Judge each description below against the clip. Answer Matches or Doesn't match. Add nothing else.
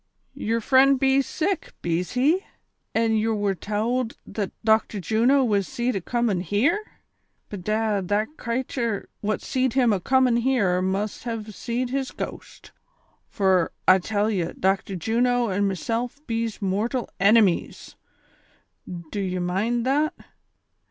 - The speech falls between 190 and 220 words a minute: Doesn't match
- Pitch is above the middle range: Matches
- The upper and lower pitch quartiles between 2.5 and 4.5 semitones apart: Matches